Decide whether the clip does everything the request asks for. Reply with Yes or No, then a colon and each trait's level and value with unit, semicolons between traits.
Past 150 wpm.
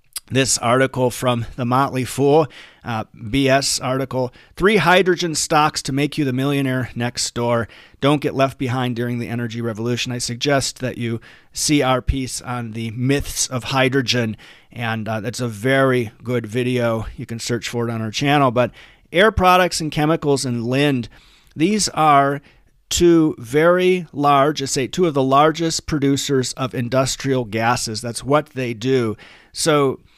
Yes: average, 160 wpm